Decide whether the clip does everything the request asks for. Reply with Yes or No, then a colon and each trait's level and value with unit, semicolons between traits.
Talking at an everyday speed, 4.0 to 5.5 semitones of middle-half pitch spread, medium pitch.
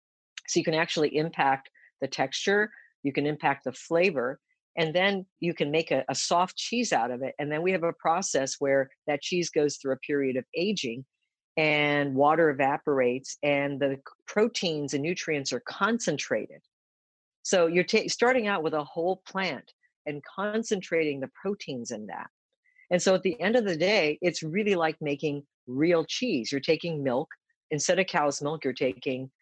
Yes: average, 175 wpm; average, 4.7 semitones; medium, 160 Hz